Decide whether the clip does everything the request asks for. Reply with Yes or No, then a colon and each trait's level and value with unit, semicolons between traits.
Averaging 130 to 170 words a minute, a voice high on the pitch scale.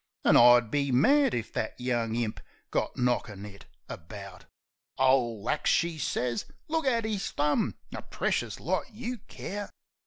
No: average, 150 wpm; low, 125 Hz